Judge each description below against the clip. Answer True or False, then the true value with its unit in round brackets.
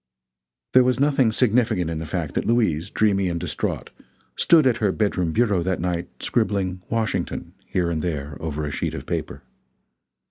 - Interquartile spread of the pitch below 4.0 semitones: False (5.1 semitones)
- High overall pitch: False (95 Hz)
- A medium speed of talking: True (170 wpm)